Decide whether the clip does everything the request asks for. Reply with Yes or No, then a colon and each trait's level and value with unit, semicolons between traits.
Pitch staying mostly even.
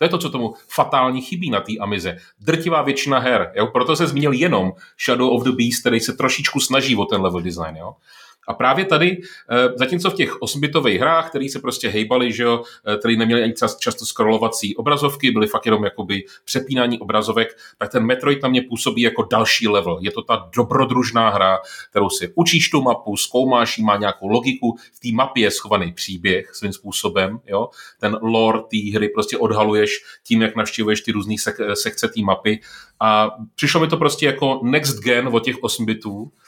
No: average, 3.9 semitones